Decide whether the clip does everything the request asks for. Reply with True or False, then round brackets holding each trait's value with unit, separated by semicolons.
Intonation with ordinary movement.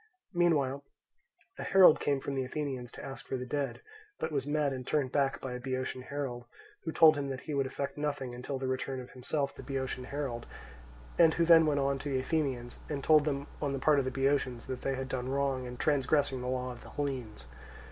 False (2.1 semitones)